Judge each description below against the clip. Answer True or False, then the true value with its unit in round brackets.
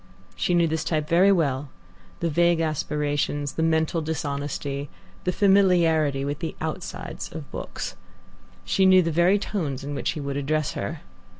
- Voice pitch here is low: False (160 Hz)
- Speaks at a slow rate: False (160 wpm)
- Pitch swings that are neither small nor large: True (3.0 semitones)